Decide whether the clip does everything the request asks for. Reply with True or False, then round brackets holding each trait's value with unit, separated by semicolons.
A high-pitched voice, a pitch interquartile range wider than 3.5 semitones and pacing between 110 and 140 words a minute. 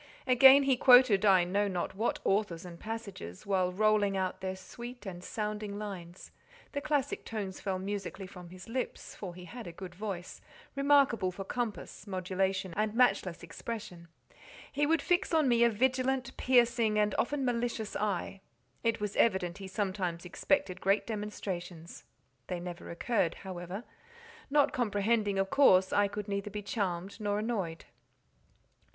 False (205 Hz; 4.0 semitones; 150 wpm)